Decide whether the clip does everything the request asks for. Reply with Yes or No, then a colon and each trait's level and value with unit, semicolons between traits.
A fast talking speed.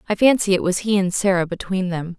Yes: fast, 245 wpm